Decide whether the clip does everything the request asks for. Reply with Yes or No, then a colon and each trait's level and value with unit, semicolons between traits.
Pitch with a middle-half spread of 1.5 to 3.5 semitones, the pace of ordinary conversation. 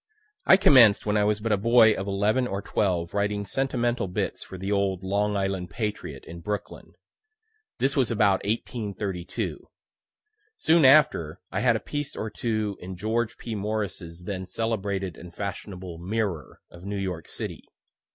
Yes: average, 2.9 semitones; average, 160 wpm